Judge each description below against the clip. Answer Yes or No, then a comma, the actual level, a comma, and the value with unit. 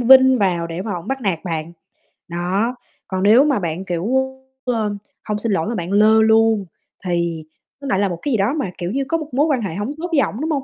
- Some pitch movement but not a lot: No, wide, 6.6 semitones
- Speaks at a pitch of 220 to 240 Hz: No, high, 210 Hz